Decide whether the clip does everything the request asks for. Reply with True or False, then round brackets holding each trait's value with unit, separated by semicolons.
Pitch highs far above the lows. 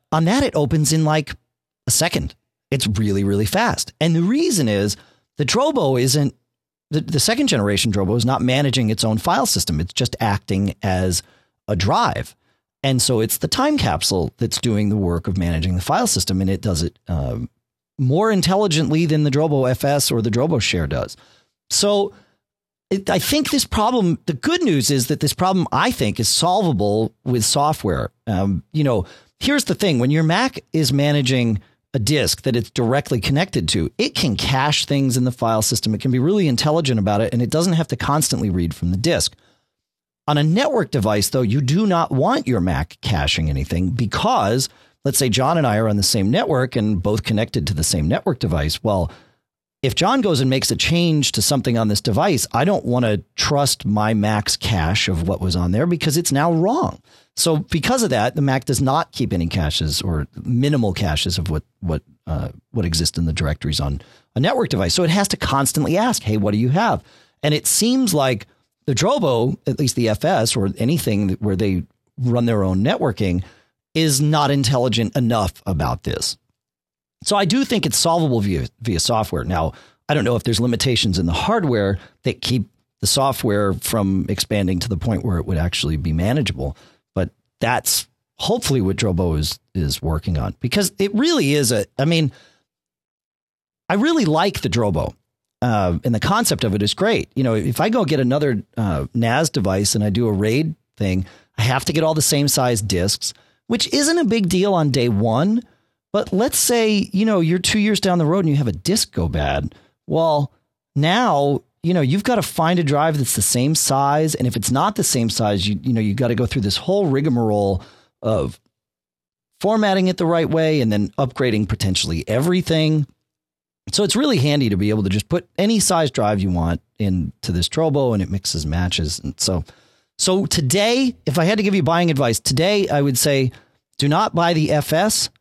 True (7.5 semitones)